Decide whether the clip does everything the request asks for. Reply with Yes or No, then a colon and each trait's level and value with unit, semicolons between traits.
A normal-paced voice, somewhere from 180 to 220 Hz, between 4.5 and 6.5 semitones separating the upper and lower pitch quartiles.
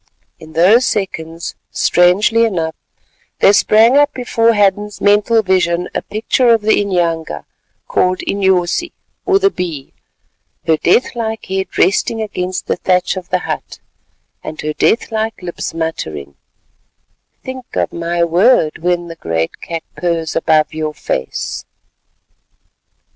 No: slow, 130 wpm; medium, 185 Hz; average, 4.9 semitones